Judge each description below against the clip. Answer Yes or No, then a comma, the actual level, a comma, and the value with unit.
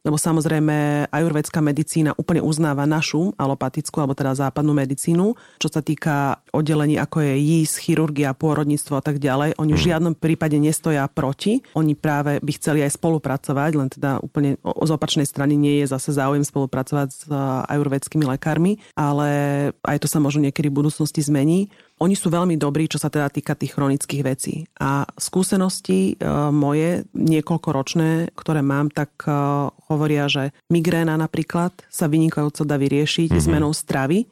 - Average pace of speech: Yes, average, 155 wpm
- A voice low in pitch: No, medium, 150 Hz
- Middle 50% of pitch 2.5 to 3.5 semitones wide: No, narrow, 2.0 semitones